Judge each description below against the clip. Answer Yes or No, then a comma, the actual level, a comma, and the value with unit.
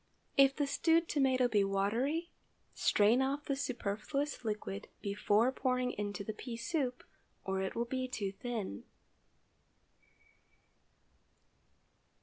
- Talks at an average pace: No, slow, 115 wpm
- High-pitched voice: Yes, high, 245 Hz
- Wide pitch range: No, average, 4.9 semitones